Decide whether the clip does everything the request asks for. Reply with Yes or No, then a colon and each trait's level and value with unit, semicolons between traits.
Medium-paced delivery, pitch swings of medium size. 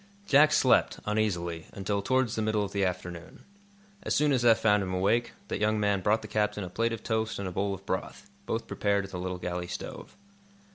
No: fast, 220 wpm; average, 3.1 semitones